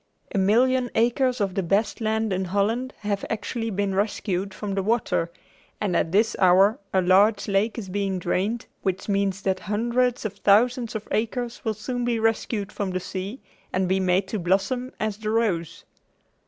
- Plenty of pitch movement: No, average, 3.0 semitones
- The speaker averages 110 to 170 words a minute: No, average, 180 wpm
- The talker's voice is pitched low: No, high, 205 Hz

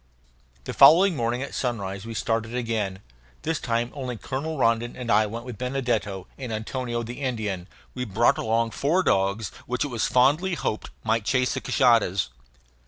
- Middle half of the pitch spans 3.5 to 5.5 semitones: No, average, 2.8 semitones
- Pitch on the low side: Yes, low, 120 Hz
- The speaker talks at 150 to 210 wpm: Yes, average, 170 wpm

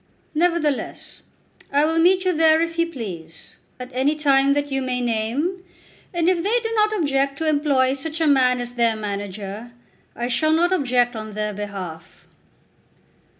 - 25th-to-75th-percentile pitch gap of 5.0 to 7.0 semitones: Yes, wide, 5.5 semitones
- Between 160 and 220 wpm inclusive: Yes, average, 165 wpm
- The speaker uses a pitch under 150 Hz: No, very high, 275 Hz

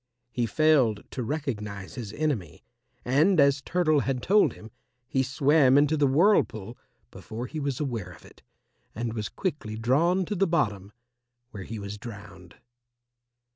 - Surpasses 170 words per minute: No, average, 150 wpm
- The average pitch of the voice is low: Yes, low, 130 Hz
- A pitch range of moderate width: No, wide, 6.0 semitones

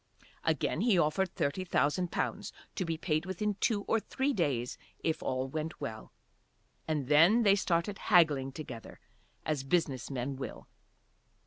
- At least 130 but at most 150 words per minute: Yes, average, 145 wpm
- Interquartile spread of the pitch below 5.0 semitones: No, wide, 5.5 semitones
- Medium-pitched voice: Yes, medium, 160 Hz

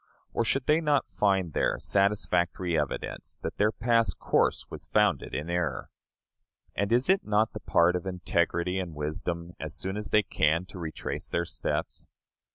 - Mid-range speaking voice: No, very low, 90 Hz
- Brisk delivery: No, average, 165 wpm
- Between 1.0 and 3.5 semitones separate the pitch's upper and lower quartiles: No, average, 3.9 semitones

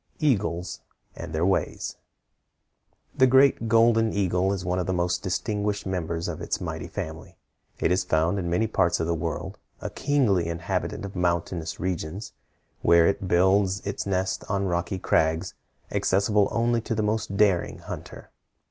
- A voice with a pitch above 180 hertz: No, very low, 95 Hz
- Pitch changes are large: No, average, 3.3 semitones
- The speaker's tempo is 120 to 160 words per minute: Yes, average, 155 wpm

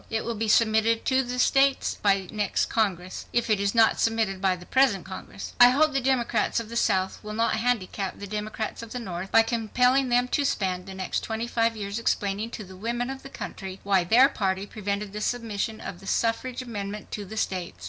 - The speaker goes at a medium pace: No, fast, 220 wpm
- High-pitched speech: Yes, high, 220 Hz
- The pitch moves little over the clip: No, average, 3.4 semitones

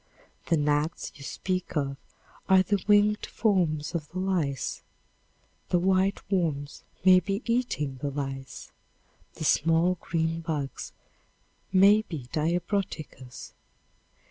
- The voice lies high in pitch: No, medium, 165 Hz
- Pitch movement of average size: Yes, average, 4.4 semitones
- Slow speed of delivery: Yes, slow, 115 wpm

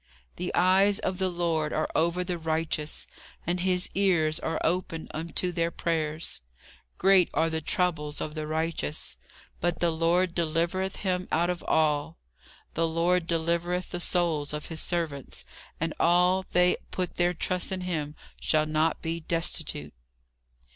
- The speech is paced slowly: No, average, 155 wpm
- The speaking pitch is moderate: Yes, medium, 170 Hz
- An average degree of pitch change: No, narrow, 2.2 semitones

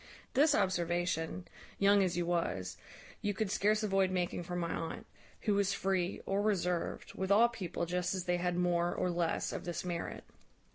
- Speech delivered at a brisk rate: No, average, 180 wpm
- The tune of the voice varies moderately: No, narrow, 2.3 semitones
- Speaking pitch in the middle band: Yes, medium, 180 Hz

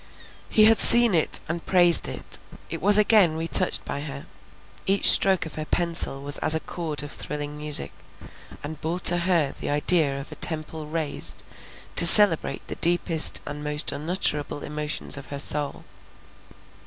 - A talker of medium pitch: Yes, medium, 155 Hz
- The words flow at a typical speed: Yes, average, 165 wpm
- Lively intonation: No, average, 3.0 semitones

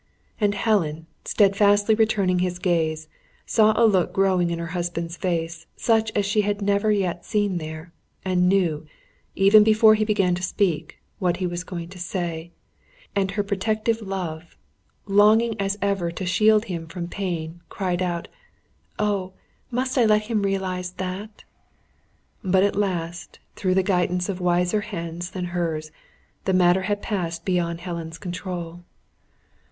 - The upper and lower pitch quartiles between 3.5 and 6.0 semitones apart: No, average, 3.0 semitones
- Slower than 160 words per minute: Yes, average, 150 wpm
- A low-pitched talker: No, medium, 185 Hz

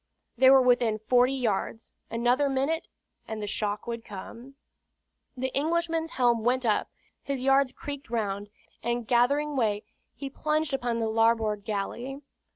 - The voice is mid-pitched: No, high, 245 Hz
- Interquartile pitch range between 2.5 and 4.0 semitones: Yes, average, 3.4 semitones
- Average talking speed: Yes, average, 145 wpm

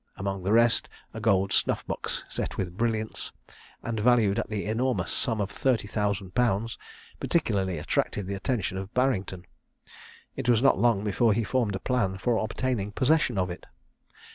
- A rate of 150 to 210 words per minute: Yes, average, 165 wpm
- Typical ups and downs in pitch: Yes, average, 3.7 semitones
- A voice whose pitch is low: Yes, low, 110 Hz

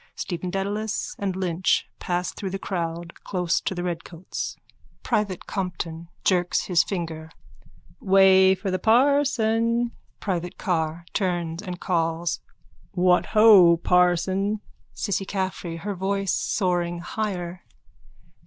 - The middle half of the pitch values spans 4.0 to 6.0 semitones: No, narrow, 2.4 semitones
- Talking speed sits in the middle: No, slow, 115 wpm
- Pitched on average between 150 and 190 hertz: Yes, medium, 185 Hz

